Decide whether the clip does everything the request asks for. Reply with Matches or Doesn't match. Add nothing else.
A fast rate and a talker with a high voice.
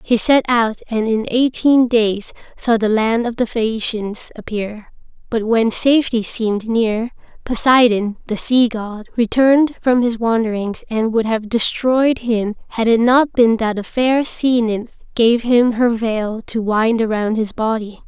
Doesn't match